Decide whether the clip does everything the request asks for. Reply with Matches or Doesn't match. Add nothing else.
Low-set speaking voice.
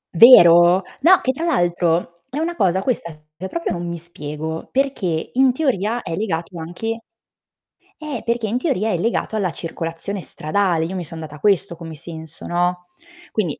Doesn't match